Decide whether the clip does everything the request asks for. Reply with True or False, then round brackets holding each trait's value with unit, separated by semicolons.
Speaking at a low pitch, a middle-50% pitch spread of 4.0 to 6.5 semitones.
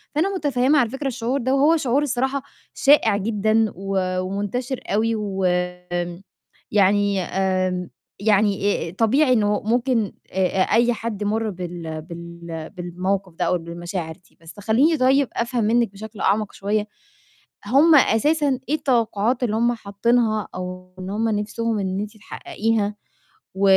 False (210 Hz; 4.4 semitones)